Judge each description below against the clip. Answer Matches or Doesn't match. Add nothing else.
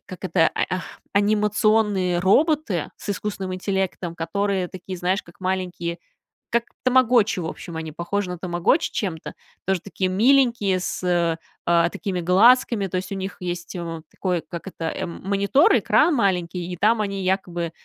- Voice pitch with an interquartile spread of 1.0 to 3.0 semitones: Matches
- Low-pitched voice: Doesn't match